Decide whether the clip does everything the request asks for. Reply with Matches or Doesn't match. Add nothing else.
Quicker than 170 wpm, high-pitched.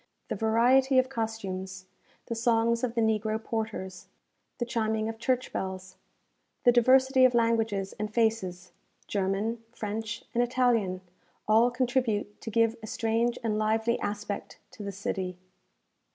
Doesn't match